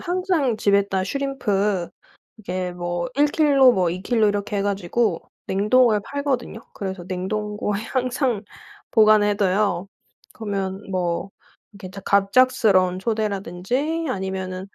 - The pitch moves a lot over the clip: No, average, 4.5 semitones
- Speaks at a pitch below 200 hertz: No, high, 205 Hz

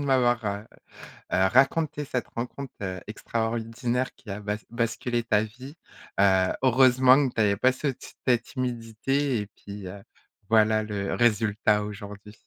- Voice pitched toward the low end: Yes, low, 115 Hz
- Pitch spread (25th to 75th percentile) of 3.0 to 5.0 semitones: Yes, average, 3.5 semitones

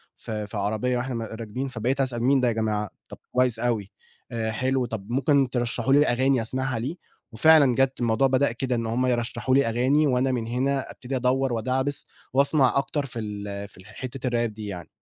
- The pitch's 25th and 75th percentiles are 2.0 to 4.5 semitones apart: Yes, average, 2.9 semitones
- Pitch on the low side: Yes, low, 125 Hz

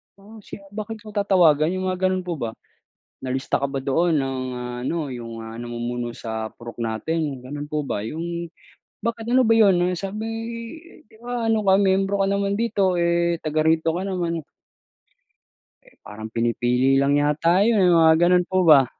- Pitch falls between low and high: Yes, medium, 170 Hz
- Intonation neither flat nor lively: No, wide, 6.3 semitones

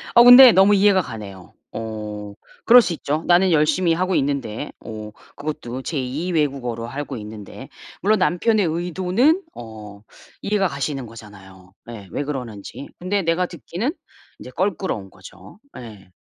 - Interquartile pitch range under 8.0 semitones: No, wide, 8.9 semitones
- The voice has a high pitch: No, medium, 145 Hz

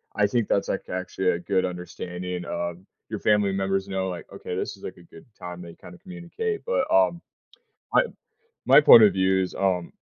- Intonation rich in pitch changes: No, average, 3.4 semitones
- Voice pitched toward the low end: Yes, very low, 95 Hz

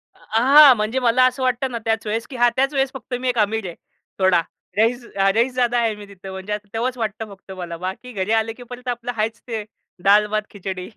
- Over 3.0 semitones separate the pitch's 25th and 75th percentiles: Yes, average, 3.5 semitones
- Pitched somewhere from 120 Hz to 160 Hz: No, high, 225 Hz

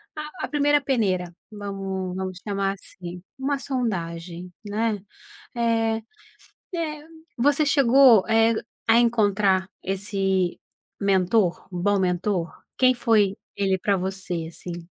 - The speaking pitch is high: Yes, high, 200 Hz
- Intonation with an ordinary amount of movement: Yes, average, 3.9 semitones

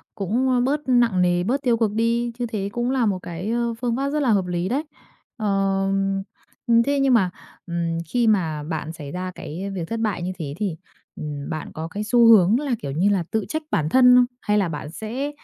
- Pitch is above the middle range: Yes, high, 210 Hz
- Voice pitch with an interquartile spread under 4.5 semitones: No, wide, 5.4 semitones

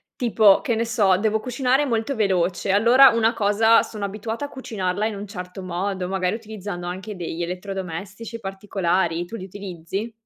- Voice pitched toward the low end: No, high, 200 Hz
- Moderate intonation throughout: Yes, average, 3.4 semitones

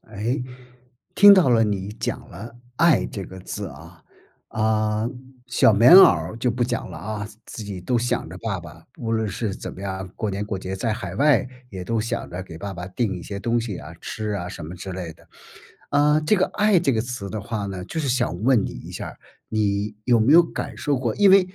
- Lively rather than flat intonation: No, average, 4.1 semitones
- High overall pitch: No, low, 110 Hz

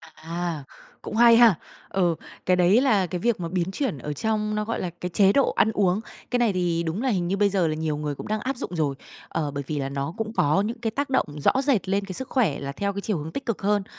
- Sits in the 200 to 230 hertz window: No, high, 190 Hz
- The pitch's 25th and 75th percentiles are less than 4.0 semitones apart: No, average, 5.1 semitones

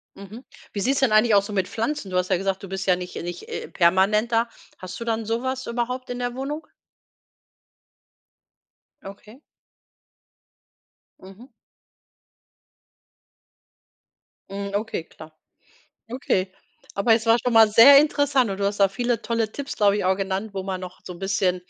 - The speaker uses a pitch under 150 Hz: No, high, 210 Hz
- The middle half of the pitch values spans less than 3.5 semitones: No, average, 3.8 semitones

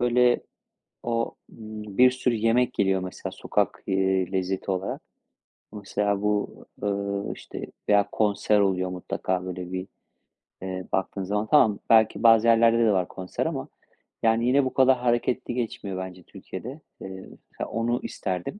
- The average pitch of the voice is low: Yes, low, 105 Hz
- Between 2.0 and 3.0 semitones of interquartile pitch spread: No, average, 3.6 semitones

